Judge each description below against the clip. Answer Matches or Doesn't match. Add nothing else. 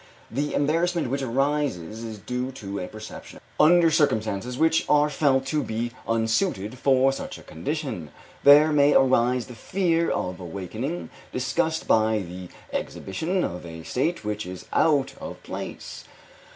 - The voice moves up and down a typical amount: Doesn't match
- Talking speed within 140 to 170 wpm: Matches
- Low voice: Matches